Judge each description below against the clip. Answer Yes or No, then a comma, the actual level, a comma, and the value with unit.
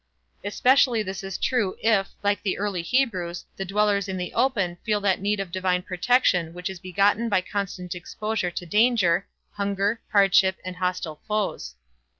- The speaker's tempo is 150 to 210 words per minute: Yes, average, 160 wpm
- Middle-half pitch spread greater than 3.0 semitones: No, narrow, 2.6 semitones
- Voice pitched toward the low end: No, high, 195 Hz